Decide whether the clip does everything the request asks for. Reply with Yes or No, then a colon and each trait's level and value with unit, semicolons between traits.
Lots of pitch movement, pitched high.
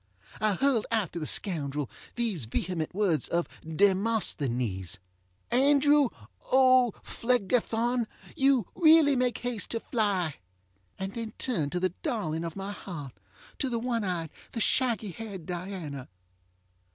Yes: wide, 6.4 semitones; high, 205 Hz